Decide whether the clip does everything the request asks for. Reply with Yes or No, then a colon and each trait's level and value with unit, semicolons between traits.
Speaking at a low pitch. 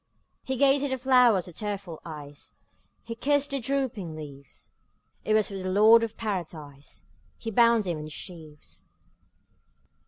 No: high, 205 Hz